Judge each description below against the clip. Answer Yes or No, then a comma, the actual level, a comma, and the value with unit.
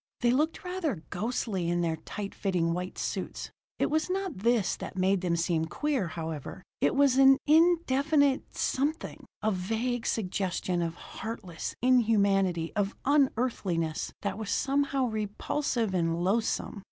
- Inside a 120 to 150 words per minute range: Yes, average, 140 wpm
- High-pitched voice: Yes, high, 215 Hz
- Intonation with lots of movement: Yes, wide, 7.0 semitones